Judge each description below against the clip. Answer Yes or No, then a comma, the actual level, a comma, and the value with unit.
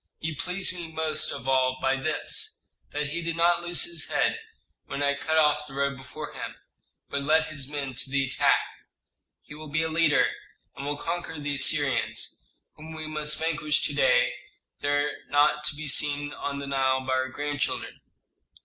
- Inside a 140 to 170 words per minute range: No, average, 190 wpm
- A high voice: No, medium, 145 Hz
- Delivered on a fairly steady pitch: Yes, narrow, 2.3 semitones